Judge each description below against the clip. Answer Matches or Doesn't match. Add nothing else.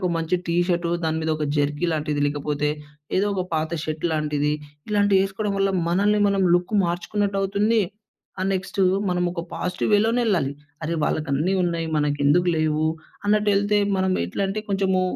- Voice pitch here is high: Doesn't match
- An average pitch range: Matches